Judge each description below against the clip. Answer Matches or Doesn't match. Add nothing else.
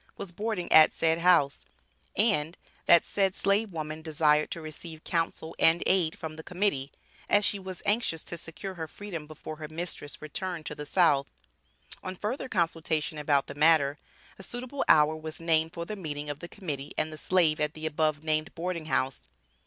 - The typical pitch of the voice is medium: Matches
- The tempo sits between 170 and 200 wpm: Matches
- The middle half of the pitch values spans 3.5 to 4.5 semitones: Doesn't match